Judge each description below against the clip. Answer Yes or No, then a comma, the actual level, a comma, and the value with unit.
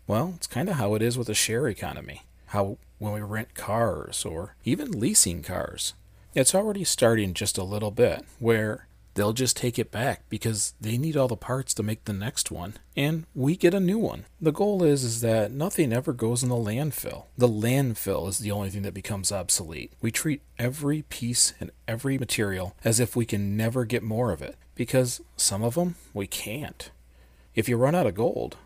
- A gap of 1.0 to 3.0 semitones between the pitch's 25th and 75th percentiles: No, average, 4.6 semitones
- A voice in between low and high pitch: No, low, 115 Hz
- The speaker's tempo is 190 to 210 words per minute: Yes, fast, 205 wpm